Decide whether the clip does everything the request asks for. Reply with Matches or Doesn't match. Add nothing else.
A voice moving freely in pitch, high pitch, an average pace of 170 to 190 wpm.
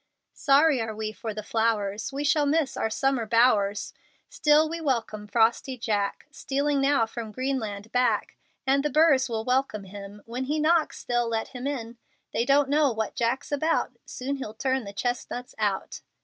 Doesn't match